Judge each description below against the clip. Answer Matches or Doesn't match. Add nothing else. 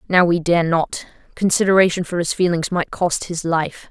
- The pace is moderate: Matches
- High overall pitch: Doesn't match